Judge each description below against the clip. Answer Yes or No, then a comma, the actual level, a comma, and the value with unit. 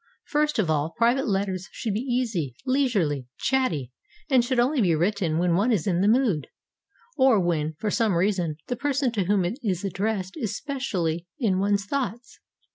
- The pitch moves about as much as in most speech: No, wide, 6.0 semitones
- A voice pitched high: Yes, high, 205 Hz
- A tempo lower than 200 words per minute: Yes, average, 180 wpm